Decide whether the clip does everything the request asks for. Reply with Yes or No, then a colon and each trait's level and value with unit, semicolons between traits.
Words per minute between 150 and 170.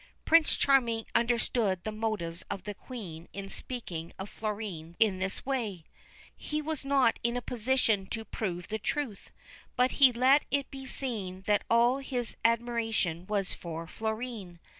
Yes: average, 155 wpm